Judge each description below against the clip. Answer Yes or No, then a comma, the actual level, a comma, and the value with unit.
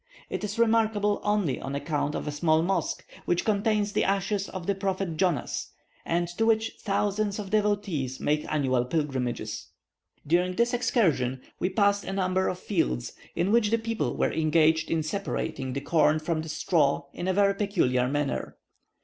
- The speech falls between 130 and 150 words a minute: No, average, 170 wpm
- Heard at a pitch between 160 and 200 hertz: Yes, medium, 185 Hz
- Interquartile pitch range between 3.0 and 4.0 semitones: No, average, 5.3 semitones